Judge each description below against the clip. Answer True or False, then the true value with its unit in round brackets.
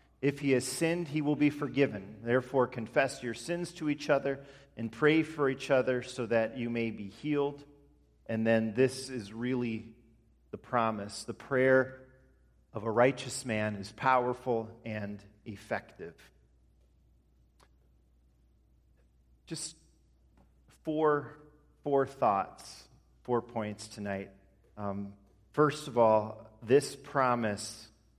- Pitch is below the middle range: True (115 Hz)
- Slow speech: True (120 wpm)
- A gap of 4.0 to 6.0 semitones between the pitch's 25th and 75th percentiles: True (5.1 semitones)